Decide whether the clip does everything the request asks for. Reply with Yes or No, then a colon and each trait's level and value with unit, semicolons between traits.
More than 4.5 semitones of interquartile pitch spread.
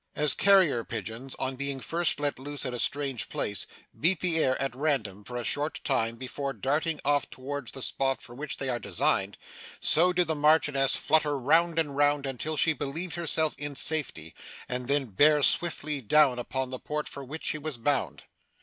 No: average, 3.0 semitones